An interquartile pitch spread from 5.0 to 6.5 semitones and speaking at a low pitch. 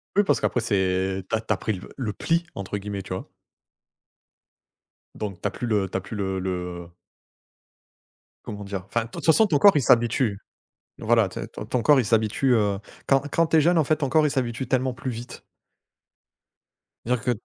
Yes: wide, 5.4 semitones; low, 115 Hz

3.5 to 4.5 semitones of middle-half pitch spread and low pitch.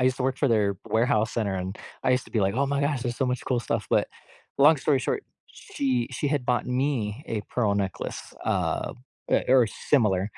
Yes: average, 4.1 semitones; low, 125 Hz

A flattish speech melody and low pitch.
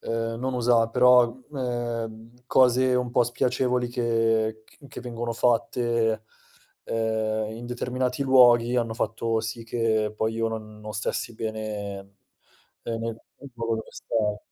Yes: narrow, 1.7 semitones; low, 115 Hz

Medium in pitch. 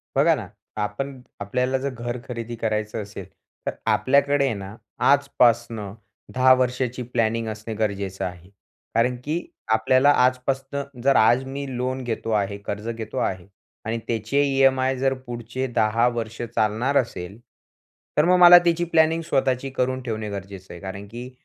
No: low, 120 Hz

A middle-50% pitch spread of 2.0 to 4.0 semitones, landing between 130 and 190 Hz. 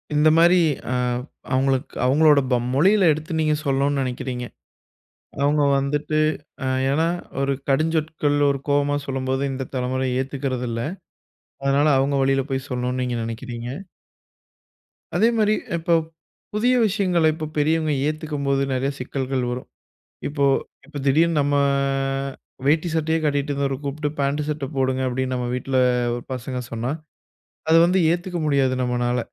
Yes: average, 3.0 semitones; medium, 140 Hz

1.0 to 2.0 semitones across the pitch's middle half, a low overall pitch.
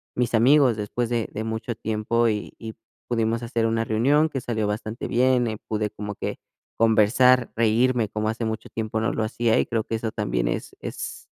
Yes: narrow, 1.7 semitones; low, 115 Hz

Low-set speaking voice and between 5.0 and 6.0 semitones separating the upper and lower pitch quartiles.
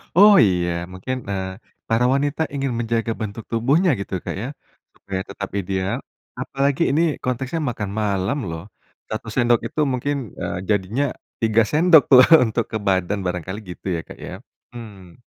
Yes: low, 115 Hz; wide, 5.4 semitones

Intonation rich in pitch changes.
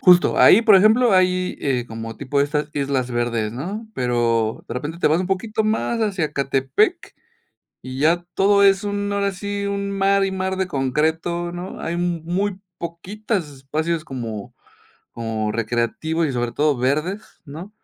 Yes: wide, 6.8 semitones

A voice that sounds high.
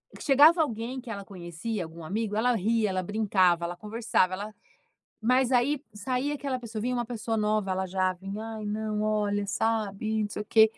Yes: high, 215 Hz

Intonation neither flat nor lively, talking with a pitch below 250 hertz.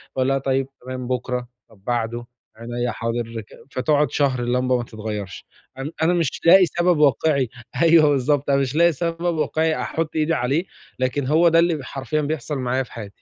Yes: average, 4.3 semitones; low, 135 Hz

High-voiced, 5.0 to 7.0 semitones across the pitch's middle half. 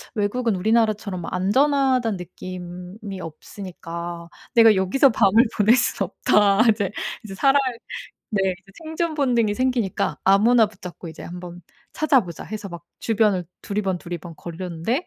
No: high, 200 Hz; average, 4.3 semitones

